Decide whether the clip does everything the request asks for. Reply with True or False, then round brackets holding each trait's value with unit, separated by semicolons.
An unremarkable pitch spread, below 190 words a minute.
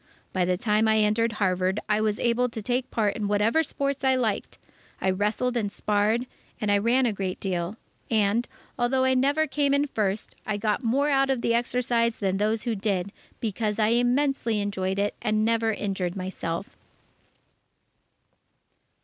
True (3.1 semitones; 170 wpm)